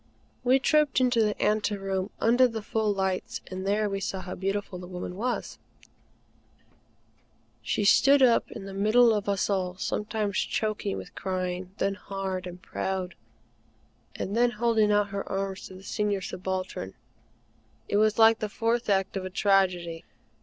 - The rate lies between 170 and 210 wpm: No, average, 160 wpm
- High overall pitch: Yes, high, 200 Hz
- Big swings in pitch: No, narrow, 2.5 semitones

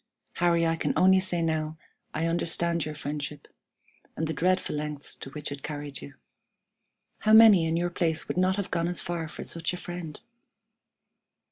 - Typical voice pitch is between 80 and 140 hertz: No, medium, 165 Hz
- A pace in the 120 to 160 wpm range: No, average, 180 wpm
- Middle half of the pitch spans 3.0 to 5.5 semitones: No, narrow, 2.5 semitones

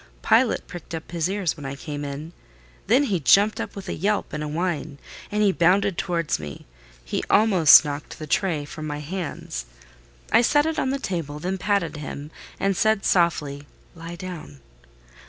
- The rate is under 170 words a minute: No, average, 175 wpm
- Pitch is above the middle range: No, medium, 170 Hz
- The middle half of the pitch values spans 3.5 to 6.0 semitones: Yes, average, 4.8 semitones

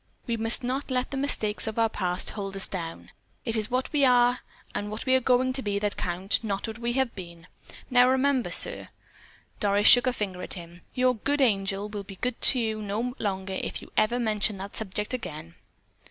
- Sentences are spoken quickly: Yes, fast, 210 wpm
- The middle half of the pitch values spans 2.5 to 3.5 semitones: No, average, 4.2 semitones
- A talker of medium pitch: No, high, 220 Hz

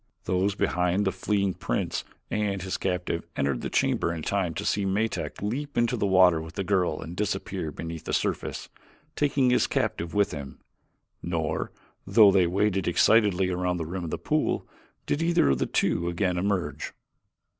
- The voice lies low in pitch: Yes, very low, 95 Hz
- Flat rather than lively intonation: No, average, 3.0 semitones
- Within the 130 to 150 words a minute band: No, average, 175 wpm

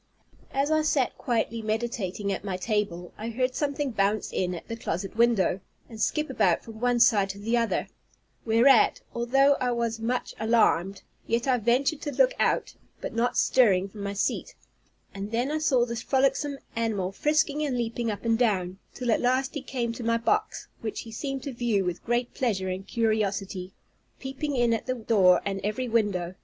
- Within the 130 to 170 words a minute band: No, average, 190 wpm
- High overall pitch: Yes, high, 230 Hz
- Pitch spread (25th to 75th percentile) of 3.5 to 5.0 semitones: Yes, average, 3.9 semitones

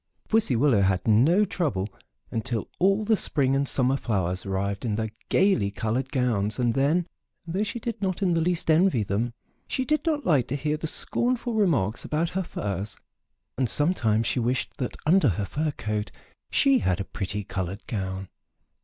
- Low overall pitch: Yes, low, 130 Hz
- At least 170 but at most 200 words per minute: Yes, average, 180 wpm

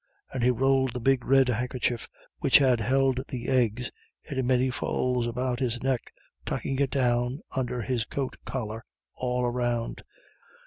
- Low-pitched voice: Yes, low, 125 Hz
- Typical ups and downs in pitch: No, narrow, 1.5 semitones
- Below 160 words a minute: Yes, average, 150 wpm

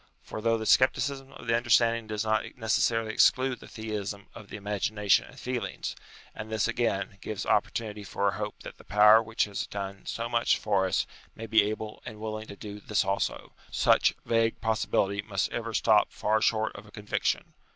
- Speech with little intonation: Yes, narrow, 1.6 semitones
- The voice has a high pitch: No, low, 110 Hz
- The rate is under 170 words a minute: No, average, 195 wpm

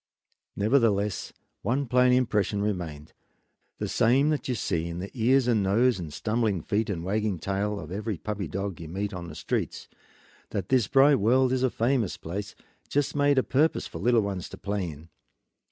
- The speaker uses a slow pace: No, average, 185 wpm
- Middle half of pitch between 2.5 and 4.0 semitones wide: No, average, 4.7 semitones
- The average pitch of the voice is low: Yes, low, 105 Hz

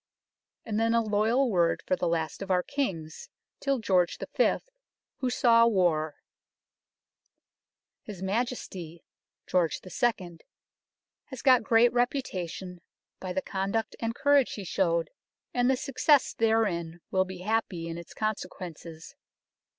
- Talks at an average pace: No, slow, 130 wpm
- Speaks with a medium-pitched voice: No, high, 195 Hz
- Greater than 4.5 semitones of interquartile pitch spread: Yes, average, 5.2 semitones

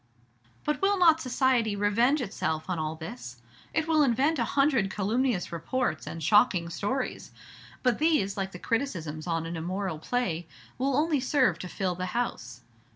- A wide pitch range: Yes, wide, 7.6 semitones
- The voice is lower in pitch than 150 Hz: No, high, 210 Hz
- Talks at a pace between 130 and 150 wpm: No, average, 160 wpm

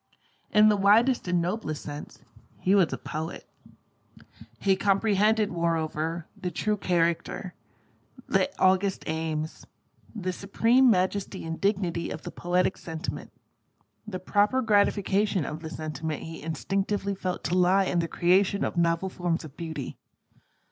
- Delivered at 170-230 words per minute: No, slow, 135 wpm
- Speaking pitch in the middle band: Yes, medium, 180 Hz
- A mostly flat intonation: No, average, 3.5 semitones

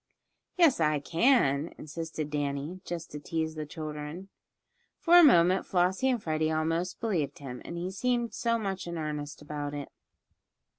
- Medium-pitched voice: Yes, medium, 165 Hz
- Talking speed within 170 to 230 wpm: No, average, 150 wpm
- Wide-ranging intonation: No, average, 4.2 semitones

